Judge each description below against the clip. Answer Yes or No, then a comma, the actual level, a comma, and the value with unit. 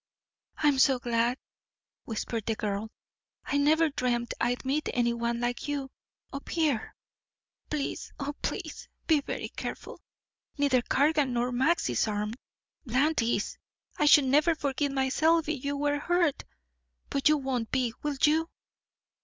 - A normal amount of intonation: Yes, average, 3.6 semitones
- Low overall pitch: No, very high, 275 Hz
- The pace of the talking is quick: No, average, 145 wpm